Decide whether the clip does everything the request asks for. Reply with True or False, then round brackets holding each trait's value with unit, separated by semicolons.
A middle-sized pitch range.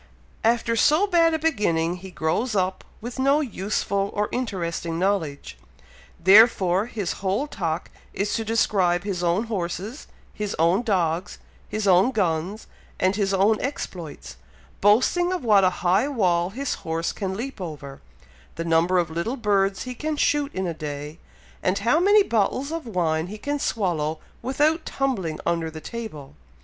False (5.7 semitones)